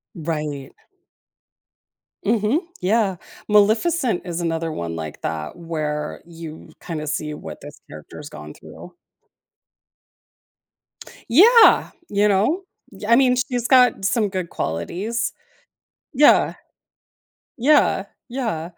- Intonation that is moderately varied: No, wide, 7.5 semitones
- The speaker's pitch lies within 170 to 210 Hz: Yes, high, 190 Hz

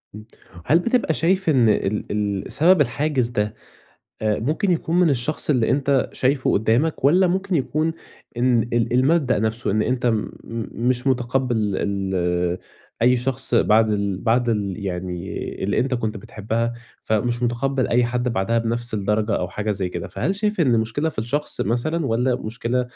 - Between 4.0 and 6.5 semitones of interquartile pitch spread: Yes, average, 4.4 semitones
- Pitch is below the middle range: Yes, low, 120 Hz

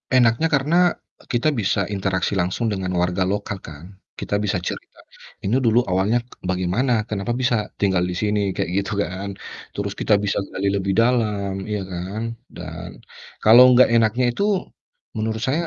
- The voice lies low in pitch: Yes, low, 105 Hz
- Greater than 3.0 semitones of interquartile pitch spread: Yes, average, 3.5 semitones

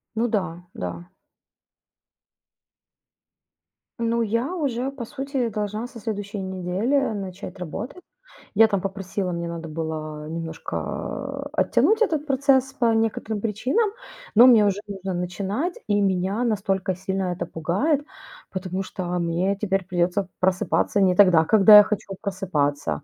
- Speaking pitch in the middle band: No, high, 195 Hz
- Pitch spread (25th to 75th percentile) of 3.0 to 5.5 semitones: Yes, average, 4.2 semitones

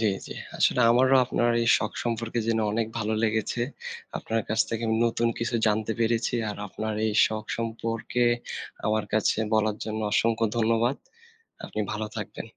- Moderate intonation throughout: No, narrow, 1.2 semitones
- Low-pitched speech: Yes, low, 115 Hz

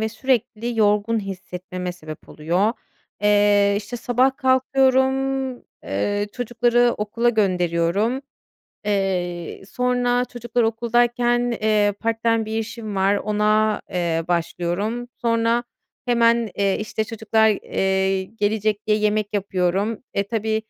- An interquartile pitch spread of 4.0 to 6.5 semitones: No, average, 3.1 semitones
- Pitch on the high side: Yes, high, 215 Hz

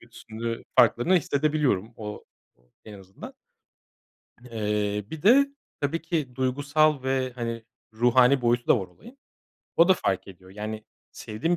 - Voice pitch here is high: No, low, 125 Hz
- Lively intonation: Yes, wide, 5.7 semitones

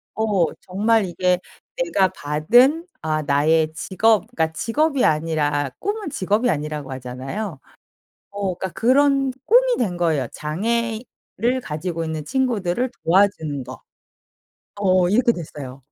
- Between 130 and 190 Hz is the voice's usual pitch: Yes, medium, 185 Hz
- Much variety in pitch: Yes, wide, 7.1 semitones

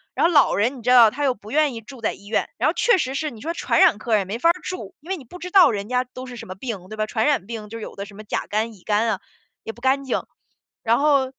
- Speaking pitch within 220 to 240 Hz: Yes, high, 235 Hz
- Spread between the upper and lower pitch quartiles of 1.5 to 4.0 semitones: No, average, 4.7 semitones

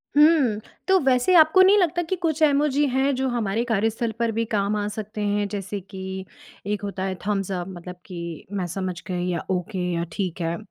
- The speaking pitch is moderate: No, high, 210 Hz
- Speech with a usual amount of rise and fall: No, wide, 6.0 semitones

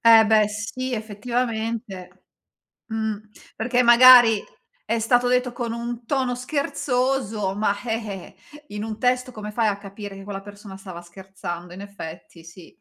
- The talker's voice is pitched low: No, high, 220 Hz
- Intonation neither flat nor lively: Yes, average, 3.6 semitones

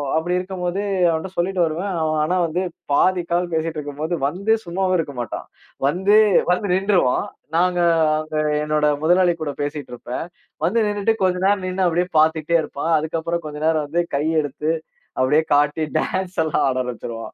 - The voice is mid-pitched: Yes, medium, 165 Hz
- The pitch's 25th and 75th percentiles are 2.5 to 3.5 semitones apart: Yes, average, 3.2 semitones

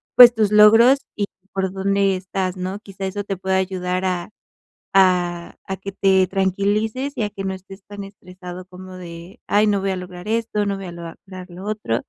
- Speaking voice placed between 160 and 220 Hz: Yes, high, 190 Hz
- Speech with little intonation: Yes, narrow, 1.9 semitones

